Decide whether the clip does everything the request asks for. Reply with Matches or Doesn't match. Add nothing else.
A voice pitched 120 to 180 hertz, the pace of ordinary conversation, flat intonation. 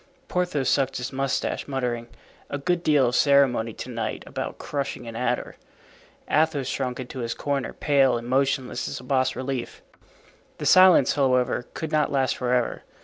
Matches